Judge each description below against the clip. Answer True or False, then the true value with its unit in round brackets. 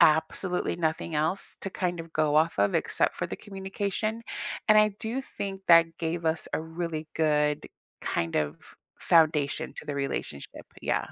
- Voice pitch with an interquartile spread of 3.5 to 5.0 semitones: True (3.9 semitones)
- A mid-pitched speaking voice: True (165 Hz)